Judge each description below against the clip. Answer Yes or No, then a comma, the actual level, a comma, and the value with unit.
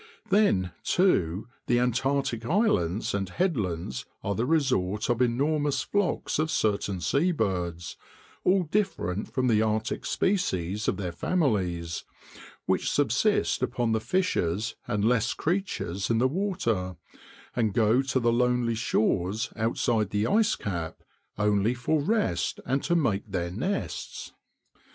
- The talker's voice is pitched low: Yes, low, 115 Hz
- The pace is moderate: No, slow, 130 wpm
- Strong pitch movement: Yes, wide, 7.1 semitones